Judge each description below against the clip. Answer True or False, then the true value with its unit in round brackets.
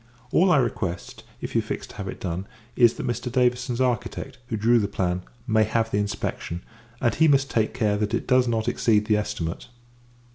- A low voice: True (115 Hz)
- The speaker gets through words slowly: False (205 wpm)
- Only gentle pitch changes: False (3.1 semitones)